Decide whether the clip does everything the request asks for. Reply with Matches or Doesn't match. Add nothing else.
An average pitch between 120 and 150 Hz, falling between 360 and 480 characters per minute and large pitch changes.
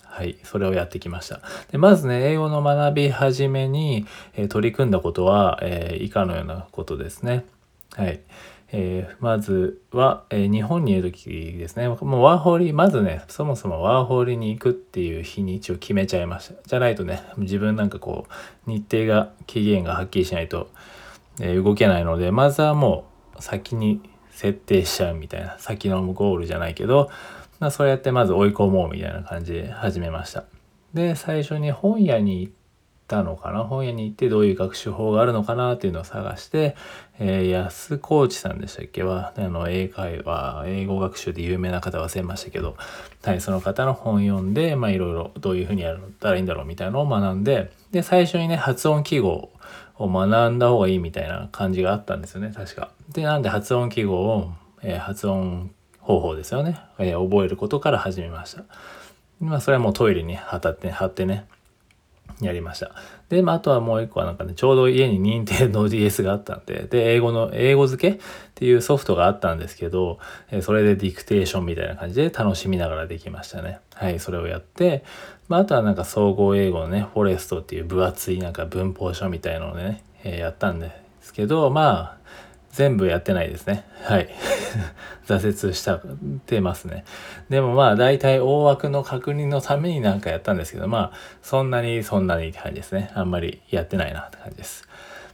Doesn't match